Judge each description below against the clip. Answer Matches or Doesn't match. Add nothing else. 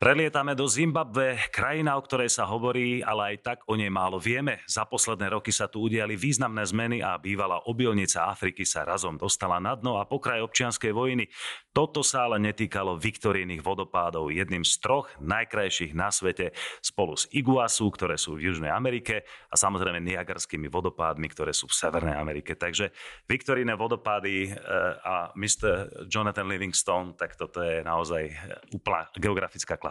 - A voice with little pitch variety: Doesn't match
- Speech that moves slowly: Doesn't match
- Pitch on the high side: Doesn't match